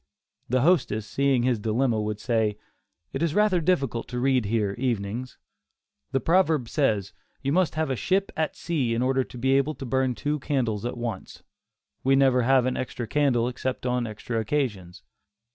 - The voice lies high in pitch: No, low, 125 Hz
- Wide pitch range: No, average, 3.3 semitones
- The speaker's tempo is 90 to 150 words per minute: No, average, 180 wpm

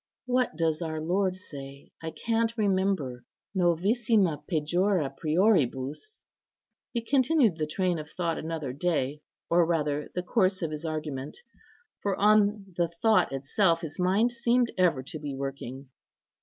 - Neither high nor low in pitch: Yes, medium, 170 Hz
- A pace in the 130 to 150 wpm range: Yes, average, 140 wpm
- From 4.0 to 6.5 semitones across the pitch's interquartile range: Yes, average, 5.2 semitones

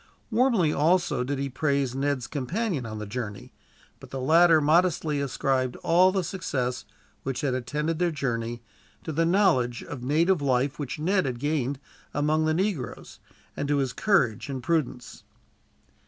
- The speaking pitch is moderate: Yes, medium, 145 Hz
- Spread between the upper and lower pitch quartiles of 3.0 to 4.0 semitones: No, average, 4.5 semitones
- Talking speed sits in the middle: Yes, average, 155 wpm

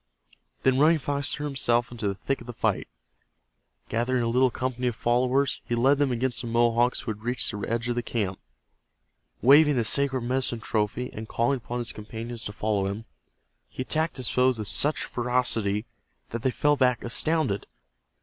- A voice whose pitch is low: Yes, low, 120 Hz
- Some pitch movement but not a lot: No, narrow, 2.3 semitones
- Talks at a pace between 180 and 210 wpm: Yes, average, 185 wpm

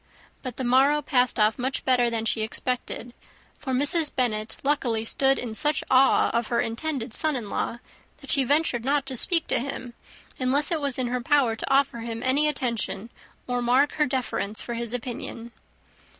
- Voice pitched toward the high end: Yes, very high, 255 Hz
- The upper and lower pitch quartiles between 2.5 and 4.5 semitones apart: Yes, average, 3.0 semitones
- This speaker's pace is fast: No, average, 185 wpm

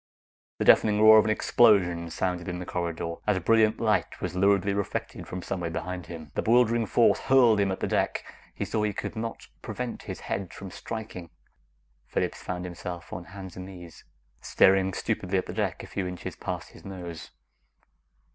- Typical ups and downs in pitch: Yes, average, 3.4 semitones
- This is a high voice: No, very low, 95 Hz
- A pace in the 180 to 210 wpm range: Yes, average, 185 wpm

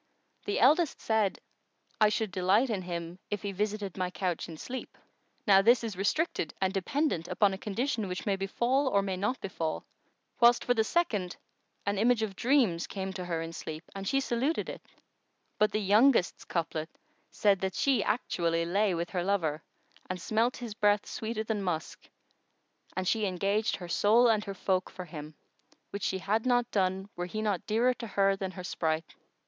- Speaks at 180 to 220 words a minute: Yes, average, 185 wpm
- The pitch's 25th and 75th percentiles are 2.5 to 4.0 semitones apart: Yes, average, 3.4 semitones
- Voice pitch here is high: Yes, high, 200 Hz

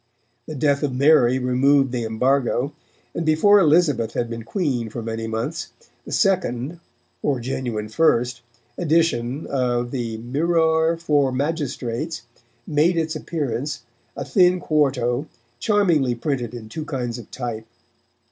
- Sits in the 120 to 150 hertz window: Yes, low, 135 Hz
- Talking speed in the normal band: No, slow, 130 wpm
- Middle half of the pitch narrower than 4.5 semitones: No, average, 4.8 semitones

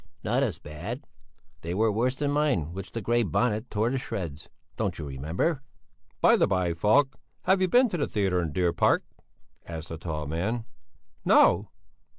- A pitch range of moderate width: No, wide, 7.1 semitones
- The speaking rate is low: No, average, 180 wpm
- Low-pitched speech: Yes, low, 100 Hz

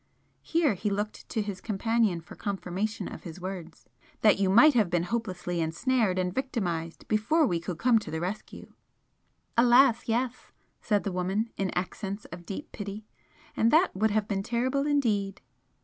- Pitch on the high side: Yes, high, 210 Hz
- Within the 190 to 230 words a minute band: No, average, 165 wpm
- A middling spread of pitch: Yes, average, 4.3 semitones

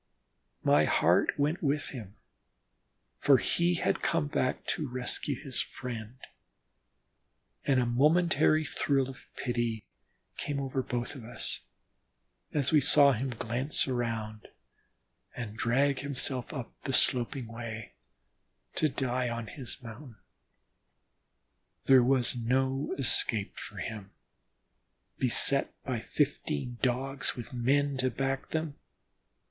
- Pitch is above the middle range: No, low, 130 Hz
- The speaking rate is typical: No, slow, 115 wpm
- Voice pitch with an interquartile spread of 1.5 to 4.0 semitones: Yes, average, 2.9 semitones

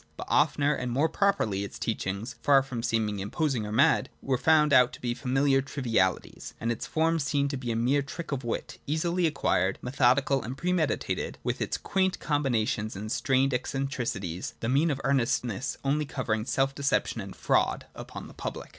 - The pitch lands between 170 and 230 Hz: No, low, 135 Hz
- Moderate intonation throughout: Yes, average, 3.8 semitones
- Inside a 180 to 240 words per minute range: Yes, average, 190 wpm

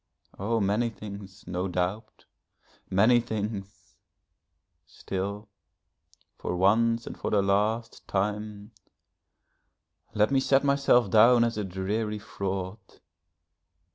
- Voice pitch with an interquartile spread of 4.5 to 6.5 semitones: No, average, 2.8 semitones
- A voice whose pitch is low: Yes, low, 105 Hz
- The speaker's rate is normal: No, slow, 105 wpm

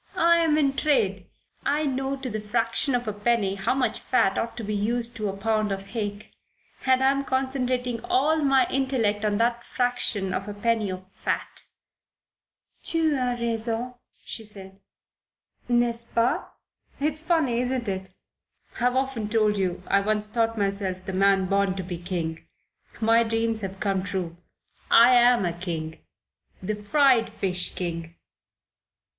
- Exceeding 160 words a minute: No, average, 155 wpm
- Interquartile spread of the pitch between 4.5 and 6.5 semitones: No, average, 4.1 semitones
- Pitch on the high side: Yes, high, 225 Hz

